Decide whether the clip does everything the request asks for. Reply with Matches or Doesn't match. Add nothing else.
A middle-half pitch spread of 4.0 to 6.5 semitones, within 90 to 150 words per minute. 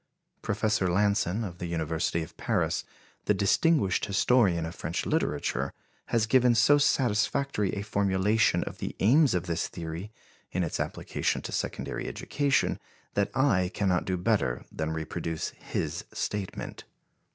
Matches